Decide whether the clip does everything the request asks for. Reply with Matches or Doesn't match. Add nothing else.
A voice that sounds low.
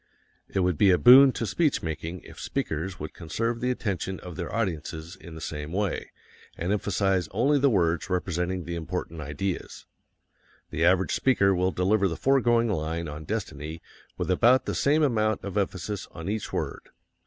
Matches